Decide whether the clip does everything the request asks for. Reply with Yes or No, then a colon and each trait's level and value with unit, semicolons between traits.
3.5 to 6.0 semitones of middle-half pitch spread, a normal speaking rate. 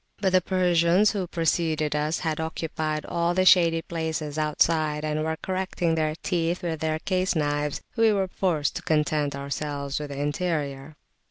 No: average, 2.7 semitones; average, 165 wpm